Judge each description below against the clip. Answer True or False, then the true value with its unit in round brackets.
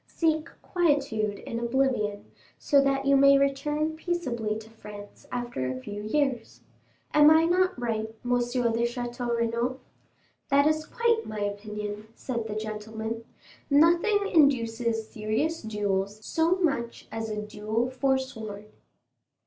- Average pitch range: True (4.7 semitones)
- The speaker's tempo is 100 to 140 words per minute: True (135 wpm)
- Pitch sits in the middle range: False (240 Hz)